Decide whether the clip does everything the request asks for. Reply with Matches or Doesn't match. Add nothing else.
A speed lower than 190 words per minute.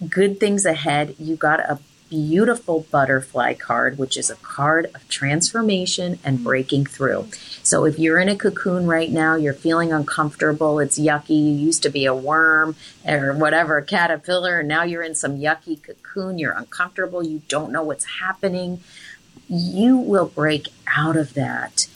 Matches